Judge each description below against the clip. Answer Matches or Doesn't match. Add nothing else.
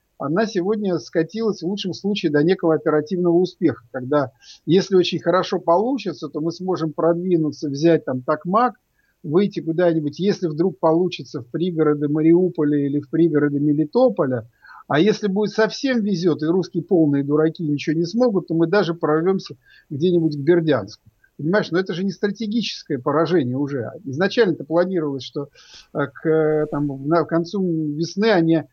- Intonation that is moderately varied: Matches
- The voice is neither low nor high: Matches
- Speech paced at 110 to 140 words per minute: Doesn't match